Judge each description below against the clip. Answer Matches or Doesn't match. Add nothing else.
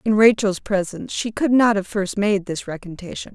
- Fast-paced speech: Doesn't match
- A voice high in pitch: Matches